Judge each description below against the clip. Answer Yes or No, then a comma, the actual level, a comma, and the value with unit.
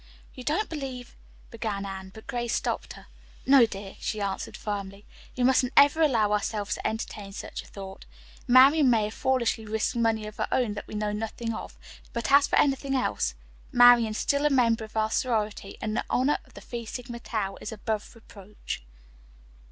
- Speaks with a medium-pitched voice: No, high, 225 Hz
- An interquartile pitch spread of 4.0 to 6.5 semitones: No, average, 3.3 semitones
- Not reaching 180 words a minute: No, average, 190 wpm